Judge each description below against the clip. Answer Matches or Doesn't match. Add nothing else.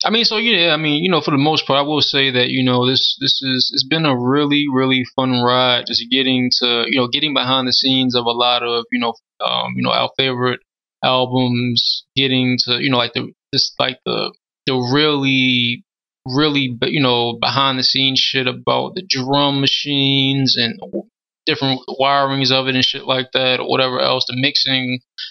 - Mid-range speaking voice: Doesn't match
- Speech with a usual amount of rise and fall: Doesn't match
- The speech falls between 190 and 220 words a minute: Matches